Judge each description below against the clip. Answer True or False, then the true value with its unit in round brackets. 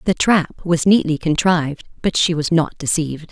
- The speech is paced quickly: False (180 wpm)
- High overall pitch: False (165 Hz)